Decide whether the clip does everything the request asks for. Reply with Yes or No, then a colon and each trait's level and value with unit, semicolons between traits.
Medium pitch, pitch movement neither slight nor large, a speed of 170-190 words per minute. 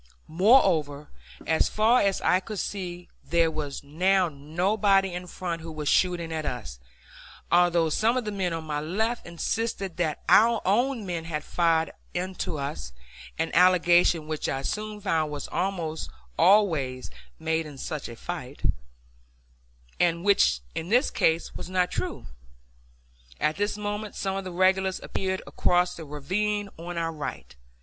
No: medium, 175 Hz; average, 3.7 semitones; average, 155 wpm